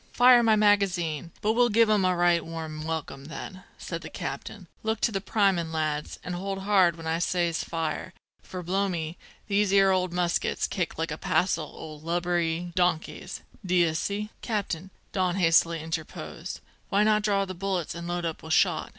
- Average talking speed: Yes, average, 180 wpm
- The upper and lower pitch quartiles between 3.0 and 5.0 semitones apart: Yes, average, 3.3 semitones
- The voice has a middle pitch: Yes, medium, 175 Hz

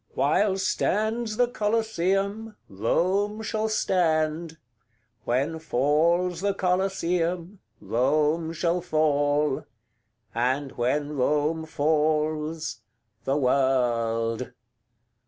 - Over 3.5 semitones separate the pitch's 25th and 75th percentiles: Yes, average, 4.9 semitones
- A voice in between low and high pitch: Yes, medium, 160 Hz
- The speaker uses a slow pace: Yes, slow, 80 wpm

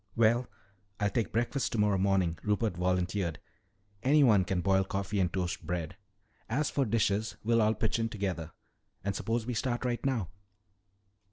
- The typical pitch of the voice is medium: No, low, 105 Hz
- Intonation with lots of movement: No, average, 3.6 semitones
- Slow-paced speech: No, average, 155 wpm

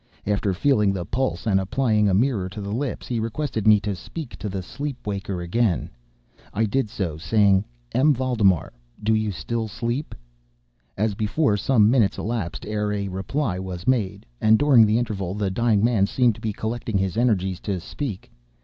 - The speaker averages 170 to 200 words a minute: Yes, average, 180 wpm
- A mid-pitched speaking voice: No, low, 105 Hz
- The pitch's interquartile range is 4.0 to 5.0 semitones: No, average, 3.5 semitones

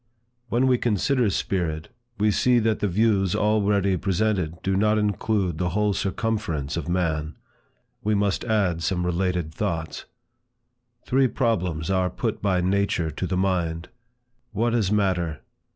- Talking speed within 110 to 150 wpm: Yes, average, 140 wpm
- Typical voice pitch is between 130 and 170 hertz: No, very low, 95 Hz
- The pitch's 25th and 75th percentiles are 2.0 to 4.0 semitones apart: Yes, average, 3.5 semitones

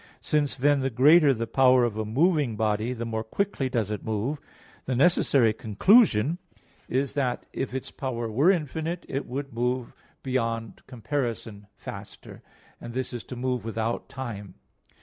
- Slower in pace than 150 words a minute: No, average, 155 wpm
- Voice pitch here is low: Yes, low, 125 Hz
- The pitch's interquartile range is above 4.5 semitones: No, average, 3.7 semitones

